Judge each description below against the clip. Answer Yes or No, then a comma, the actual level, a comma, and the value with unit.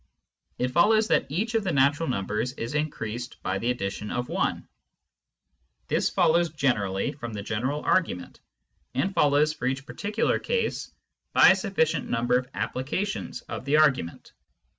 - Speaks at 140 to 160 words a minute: Yes, average, 155 wpm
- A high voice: No, medium, 140 Hz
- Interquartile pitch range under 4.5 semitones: No, wide, 5.6 semitones